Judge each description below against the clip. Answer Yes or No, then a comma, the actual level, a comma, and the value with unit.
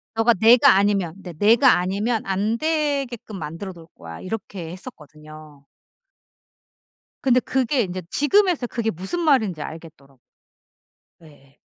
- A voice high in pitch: Yes, high, 200 Hz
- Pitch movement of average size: No, wide, 7.0 semitones